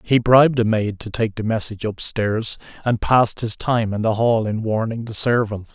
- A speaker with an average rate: No, fast, 210 wpm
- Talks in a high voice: No, low, 110 Hz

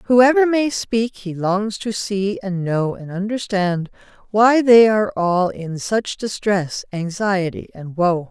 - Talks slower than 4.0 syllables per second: Yes, 3.6 syllables/s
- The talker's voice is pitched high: Yes, high, 205 Hz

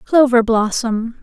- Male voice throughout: No, female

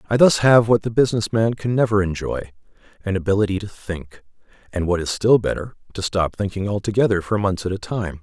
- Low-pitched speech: Yes, low, 100 Hz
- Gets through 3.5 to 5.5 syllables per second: No, 5.8 syllables/s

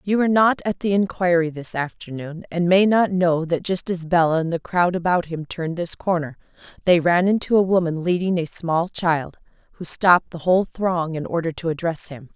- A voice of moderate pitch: Yes, medium, 175 Hz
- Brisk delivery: Yes, fast, 210 wpm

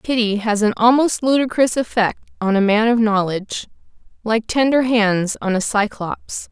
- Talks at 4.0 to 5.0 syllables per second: Yes, 4.7 syllables/s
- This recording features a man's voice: No, female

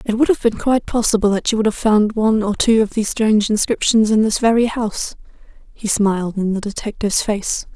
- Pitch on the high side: Yes, high, 215 Hz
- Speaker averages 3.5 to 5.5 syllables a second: No, 6.0 syllables/s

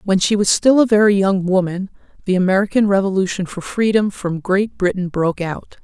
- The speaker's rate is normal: Yes, average, 185 wpm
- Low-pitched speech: No, high, 195 Hz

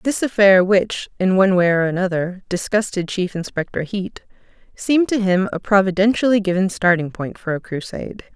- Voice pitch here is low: No, high, 190 Hz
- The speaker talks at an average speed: Yes, average, 165 wpm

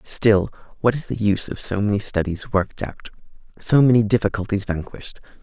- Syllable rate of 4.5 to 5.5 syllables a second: No, 6.0 syllables/s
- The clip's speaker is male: Yes, male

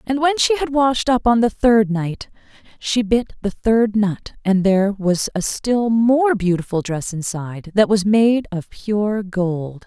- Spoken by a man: No, female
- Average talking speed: Yes, average, 180 wpm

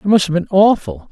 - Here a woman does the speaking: No, male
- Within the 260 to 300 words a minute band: Yes, fast, 270 wpm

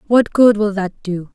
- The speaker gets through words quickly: Yes, fast, 225 wpm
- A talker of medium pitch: No, high, 205 Hz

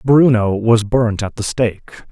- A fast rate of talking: No, average, 170 wpm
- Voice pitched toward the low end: Yes, low, 115 Hz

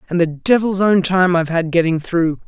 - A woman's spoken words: Yes, female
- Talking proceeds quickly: Yes, fast, 220 wpm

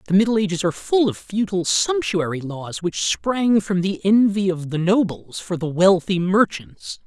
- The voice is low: No, medium, 185 Hz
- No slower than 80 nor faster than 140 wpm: No, average, 180 wpm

